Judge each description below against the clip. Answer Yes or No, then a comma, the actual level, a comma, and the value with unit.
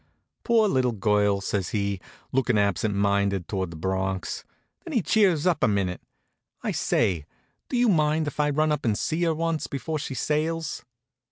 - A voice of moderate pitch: No, low, 125 Hz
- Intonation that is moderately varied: No, wide, 8.1 semitones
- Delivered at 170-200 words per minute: Yes, average, 175 wpm